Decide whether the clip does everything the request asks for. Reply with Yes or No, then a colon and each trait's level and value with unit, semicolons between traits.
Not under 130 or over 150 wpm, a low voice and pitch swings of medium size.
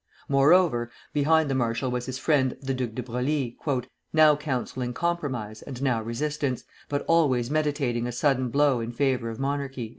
No: average, 160 wpm; low, 130 Hz; average, 3.2 semitones